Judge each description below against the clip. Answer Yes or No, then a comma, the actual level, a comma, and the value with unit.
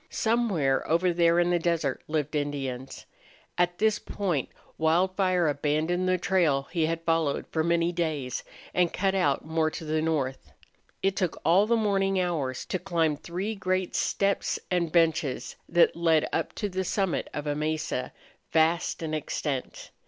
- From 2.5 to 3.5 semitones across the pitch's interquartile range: Yes, average, 3.1 semitones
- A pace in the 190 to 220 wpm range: No, average, 160 wpm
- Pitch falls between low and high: Yes, medium, 170 Hz